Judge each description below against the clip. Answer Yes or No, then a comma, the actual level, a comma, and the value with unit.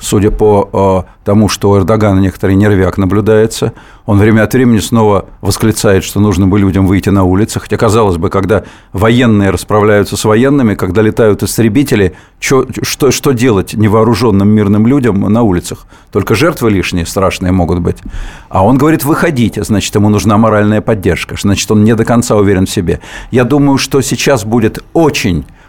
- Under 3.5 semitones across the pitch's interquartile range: Yes, average, 2.9 semitones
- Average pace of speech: No, fast, 165 wpm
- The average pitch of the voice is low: Yes, low, 105 Hz